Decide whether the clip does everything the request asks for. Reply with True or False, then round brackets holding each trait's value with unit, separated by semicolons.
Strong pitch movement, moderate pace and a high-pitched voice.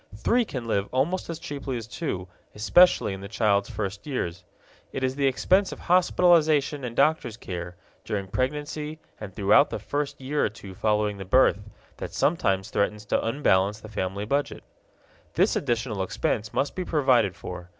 False (6.5 semitones; 170 wpm; 115 Hz)